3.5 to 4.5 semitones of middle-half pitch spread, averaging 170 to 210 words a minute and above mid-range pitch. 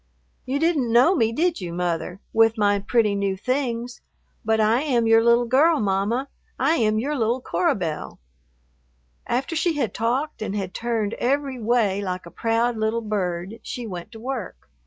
Yes: average, 3.9 semitones; average, 175 wpm; high, 230 Hz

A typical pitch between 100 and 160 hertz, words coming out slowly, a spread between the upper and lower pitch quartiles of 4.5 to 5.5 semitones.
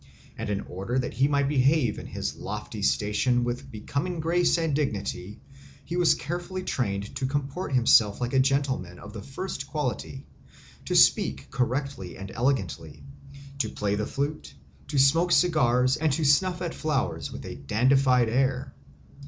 No: low, 135 Hz; average, 160 wpm; average, 5.0 semitones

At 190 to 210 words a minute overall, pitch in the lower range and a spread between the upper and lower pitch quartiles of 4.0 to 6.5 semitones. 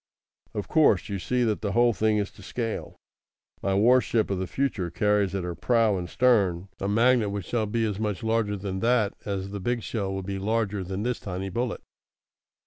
No: fast, 205 wpm; low, 105 Hz; average, 3.0 semitones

